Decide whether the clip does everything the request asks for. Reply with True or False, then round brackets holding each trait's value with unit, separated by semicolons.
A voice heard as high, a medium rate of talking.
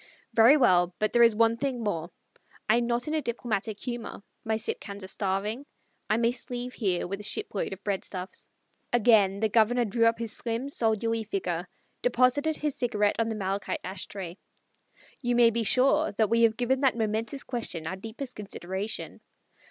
True (225 Hz; 180 wpm)